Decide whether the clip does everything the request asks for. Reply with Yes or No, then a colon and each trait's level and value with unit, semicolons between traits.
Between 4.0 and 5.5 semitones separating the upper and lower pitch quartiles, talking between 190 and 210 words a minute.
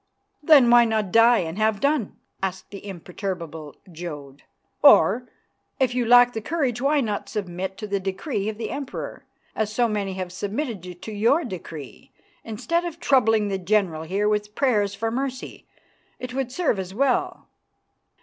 No: average, 4.4 semitones; average, 160 wpm